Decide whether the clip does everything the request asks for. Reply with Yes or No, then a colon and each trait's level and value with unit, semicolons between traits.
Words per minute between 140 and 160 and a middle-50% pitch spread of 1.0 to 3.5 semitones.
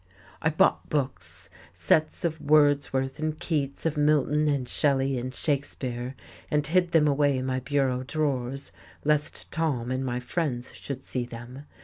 Yes: average, 150 wpm; average, 2.8 semitones